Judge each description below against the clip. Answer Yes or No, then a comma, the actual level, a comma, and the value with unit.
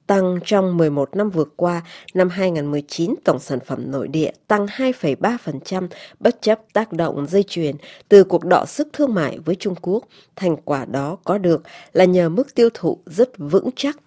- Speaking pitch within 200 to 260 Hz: No, medium, 185 Hz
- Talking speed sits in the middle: Yes, average, 185 wpm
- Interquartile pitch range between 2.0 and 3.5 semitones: No, average, 4.2 semitones